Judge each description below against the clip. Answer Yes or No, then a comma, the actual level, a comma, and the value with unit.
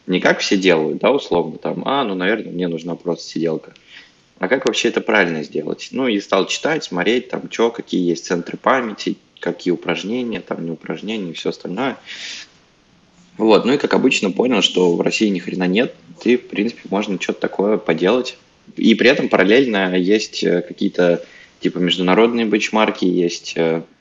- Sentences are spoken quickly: Yes, fast, 170 wpm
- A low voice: Yes, very low, 90 Hz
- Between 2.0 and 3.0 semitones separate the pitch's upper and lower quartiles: Yes, average, 2.7 semitones